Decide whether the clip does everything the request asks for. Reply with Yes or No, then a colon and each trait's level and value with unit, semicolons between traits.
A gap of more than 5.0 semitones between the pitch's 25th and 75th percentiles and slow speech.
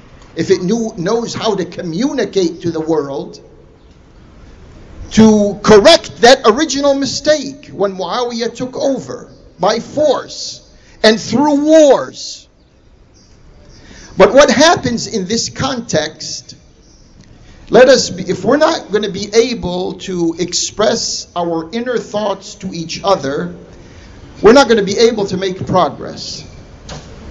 Yes: wide, 5.5 semitones; slow, 125 wpm